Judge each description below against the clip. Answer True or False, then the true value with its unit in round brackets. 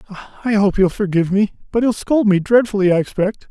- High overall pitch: True (205 Hz)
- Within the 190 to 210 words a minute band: True (205 wpm)